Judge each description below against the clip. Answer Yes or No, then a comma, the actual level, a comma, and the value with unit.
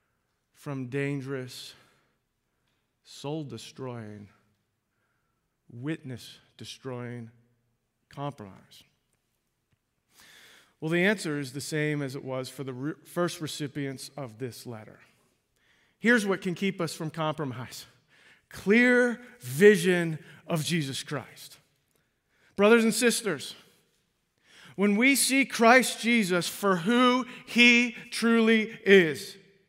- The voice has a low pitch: No, medium, 155 Hz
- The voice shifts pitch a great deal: Yes, wide, 7.8 semitones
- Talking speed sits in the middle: No, slow, 95 wpm